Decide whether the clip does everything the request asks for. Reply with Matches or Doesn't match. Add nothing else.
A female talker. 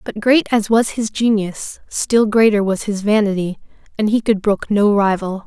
Matches